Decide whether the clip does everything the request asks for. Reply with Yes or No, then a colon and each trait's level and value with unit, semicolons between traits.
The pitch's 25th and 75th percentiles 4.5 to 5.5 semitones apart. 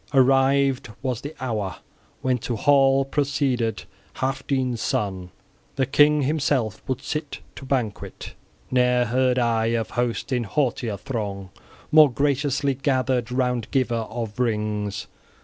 No: average, 3.1 semitones